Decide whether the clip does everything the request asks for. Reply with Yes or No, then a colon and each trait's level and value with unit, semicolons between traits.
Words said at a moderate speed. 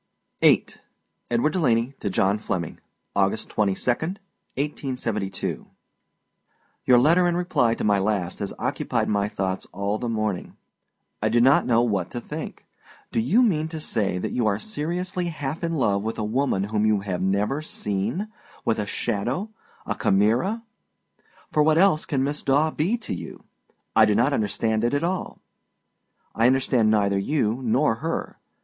Yes: average, 160 wpm